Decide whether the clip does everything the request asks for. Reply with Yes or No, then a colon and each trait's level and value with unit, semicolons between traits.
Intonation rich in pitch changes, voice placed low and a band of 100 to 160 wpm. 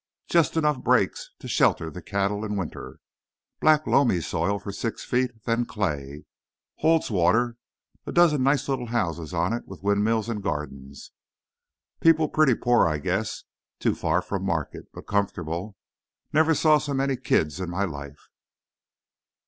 Yes: wide, 7.5 semitones; low, 105 Hz; average, 150 wpm